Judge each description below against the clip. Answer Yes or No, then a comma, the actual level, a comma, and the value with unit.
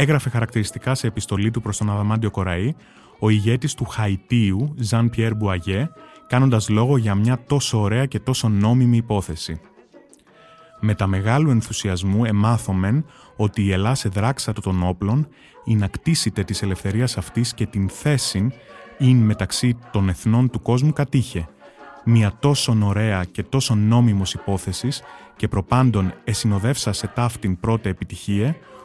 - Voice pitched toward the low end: Yes, low, 110 Hz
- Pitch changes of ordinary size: Yes, average, 4.0 semitones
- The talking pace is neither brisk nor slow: Yes, average, 140 wpm